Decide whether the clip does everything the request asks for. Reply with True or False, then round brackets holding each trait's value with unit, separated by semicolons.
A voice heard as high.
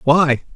False (150 Hz)